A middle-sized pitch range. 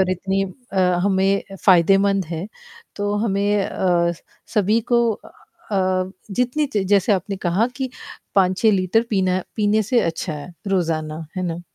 No: narrow, 2.3 semitones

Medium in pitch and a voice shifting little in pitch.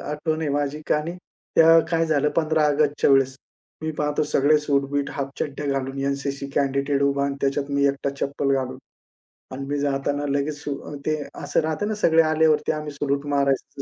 Yes: medium, 145 Hz; narrow, 1.7 semitones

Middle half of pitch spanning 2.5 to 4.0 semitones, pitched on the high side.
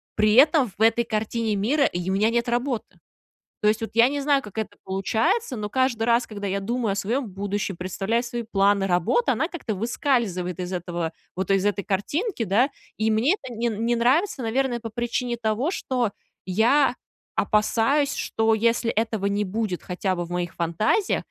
Yes: average, 3.6 semitones; high, 225 Hz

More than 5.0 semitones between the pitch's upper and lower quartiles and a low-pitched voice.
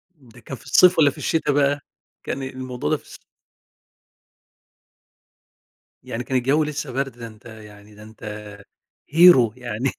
No: average, 3.9 semitones; low, 130 Hz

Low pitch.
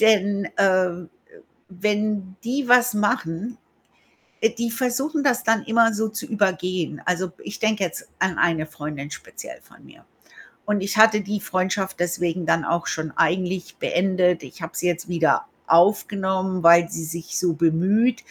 No: high, 190 Hz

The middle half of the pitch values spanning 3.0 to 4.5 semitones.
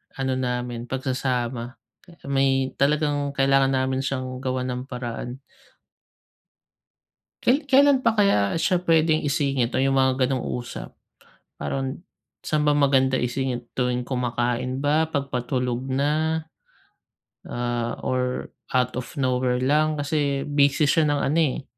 No: narrow, 2.6 semitones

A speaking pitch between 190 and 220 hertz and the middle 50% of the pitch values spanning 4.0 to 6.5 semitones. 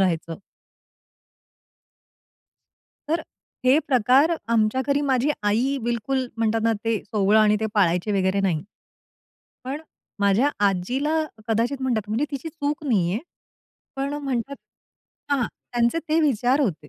No: high, 240 Hz; average, 5.0 semitones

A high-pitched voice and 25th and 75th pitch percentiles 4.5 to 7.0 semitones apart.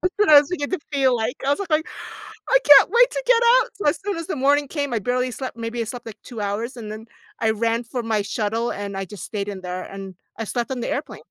Yes: high, 240 Hz; average, 5.0 semitones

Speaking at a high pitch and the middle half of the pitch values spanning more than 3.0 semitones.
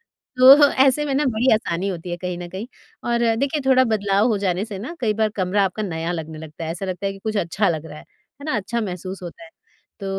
Yes: high, 200 Hz; average, 5.1 semitones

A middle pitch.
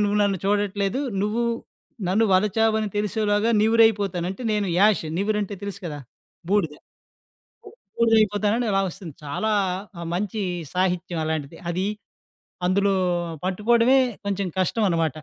No: high, 205 Hz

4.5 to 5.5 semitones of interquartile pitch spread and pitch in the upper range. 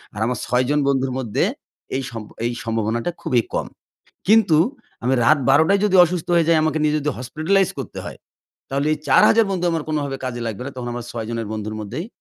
No: average, 5.1 semitones; low, 135 Hz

